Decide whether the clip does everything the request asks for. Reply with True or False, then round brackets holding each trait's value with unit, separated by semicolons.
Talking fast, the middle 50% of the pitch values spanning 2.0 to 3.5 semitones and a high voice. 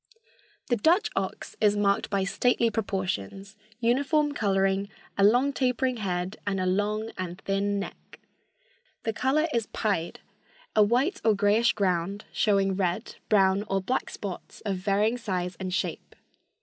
False (145 wpm; 3.2 semitones; 205 Hz)